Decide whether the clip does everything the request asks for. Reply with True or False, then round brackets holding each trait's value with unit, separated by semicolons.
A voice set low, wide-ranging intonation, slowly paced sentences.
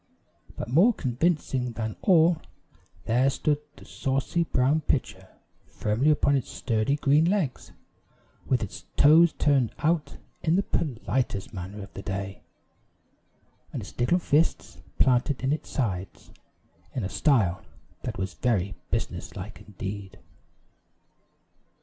True (130 Hz; 6.3 semitones; 125 wpm)